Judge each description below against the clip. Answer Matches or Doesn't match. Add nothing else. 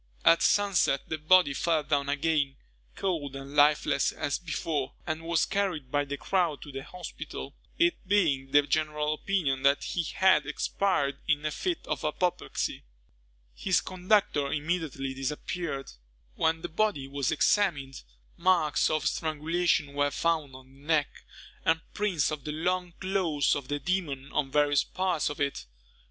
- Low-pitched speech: Doesn't match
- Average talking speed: Matches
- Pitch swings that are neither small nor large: Matches